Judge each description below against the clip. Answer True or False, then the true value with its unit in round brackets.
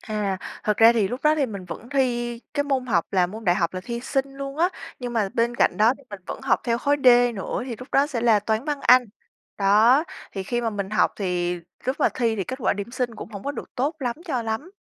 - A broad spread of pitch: False (4.2 semitones)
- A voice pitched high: True (235 Hz)